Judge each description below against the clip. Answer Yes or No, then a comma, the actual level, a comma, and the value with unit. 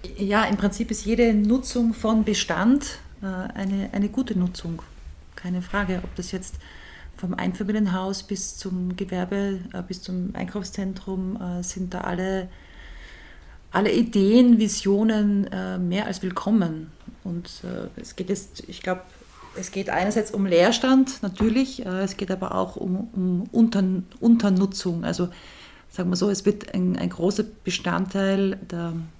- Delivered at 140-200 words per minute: No, average, 130 wpm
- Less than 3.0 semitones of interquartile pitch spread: Yes, narrow, 2.4 semitones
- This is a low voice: No, high, 195 Hz